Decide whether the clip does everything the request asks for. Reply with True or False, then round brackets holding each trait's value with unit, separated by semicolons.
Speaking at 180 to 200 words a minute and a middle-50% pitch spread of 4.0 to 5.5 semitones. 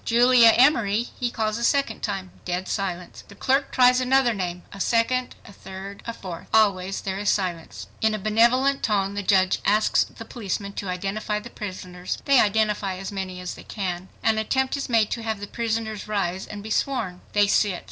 False (195 wpm; 3.4 semitones)